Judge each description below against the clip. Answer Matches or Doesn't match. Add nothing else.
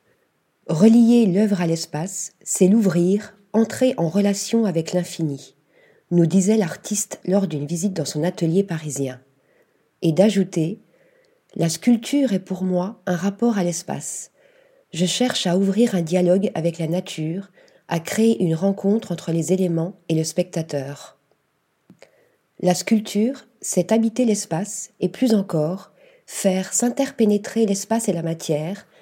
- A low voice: Doesn't match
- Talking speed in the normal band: Doesn't match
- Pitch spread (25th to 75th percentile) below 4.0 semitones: Doesn't match